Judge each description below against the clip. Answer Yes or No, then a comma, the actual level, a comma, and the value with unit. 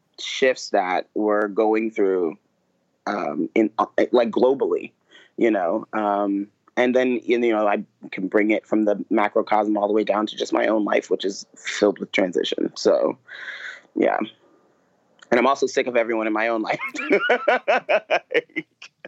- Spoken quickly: No, average, 160 wpm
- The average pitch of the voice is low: Yes, low, 110 Hz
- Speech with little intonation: Yes, narrow, 1.7 semitones